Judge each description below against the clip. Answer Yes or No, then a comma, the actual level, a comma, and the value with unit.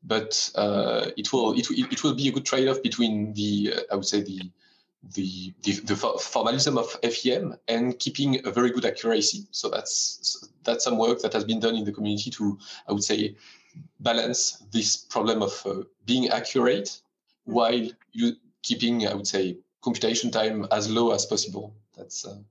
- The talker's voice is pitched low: Yes, low, 115 Hz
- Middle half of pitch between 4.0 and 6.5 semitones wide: Yes, average, 4.4 semitones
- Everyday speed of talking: Yes, average, 185 wpm